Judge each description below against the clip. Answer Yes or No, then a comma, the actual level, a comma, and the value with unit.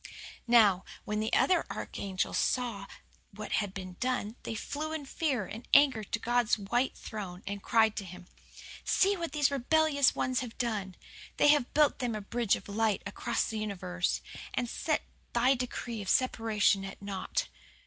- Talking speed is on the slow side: No, average, 170 wpm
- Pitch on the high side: Yes, high, 225 Hz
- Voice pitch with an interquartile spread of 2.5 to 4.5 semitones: Yes, average, 4.2 semitones